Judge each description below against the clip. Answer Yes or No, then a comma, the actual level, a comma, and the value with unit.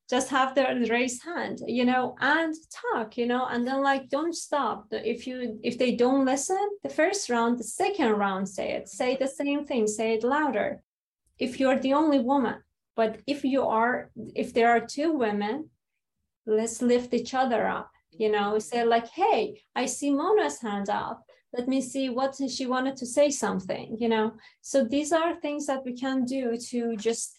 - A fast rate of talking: No, average, 190 wpm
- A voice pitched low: No, very high, 255 Hz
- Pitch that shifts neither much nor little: Yes, average, 3.2 semitones